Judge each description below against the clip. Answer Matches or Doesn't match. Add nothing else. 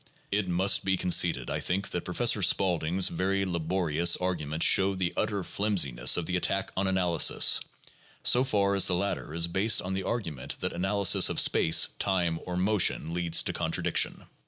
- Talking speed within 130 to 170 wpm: Doesn't match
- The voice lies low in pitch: Matches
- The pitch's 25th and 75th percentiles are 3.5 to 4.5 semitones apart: Doesn't match